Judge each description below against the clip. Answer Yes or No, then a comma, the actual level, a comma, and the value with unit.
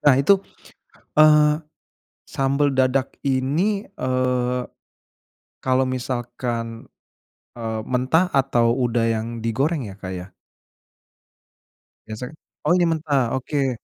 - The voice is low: Yes, low, 130 Hz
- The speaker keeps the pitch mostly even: No, average, 3.2 semitones